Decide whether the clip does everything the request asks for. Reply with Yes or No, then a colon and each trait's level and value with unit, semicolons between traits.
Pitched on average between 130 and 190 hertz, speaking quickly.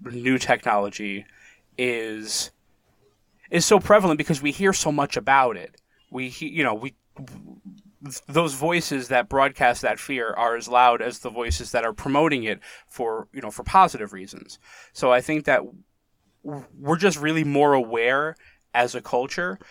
No: low, 135 Hz; average, 160 wpm